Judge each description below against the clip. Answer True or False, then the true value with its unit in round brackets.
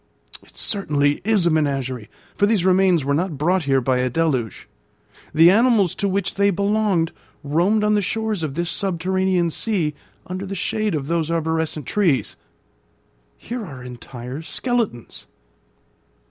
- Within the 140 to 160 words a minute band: True (145 wpm)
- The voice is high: False (170 Hz)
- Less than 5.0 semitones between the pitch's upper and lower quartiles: False (5.5 semitones)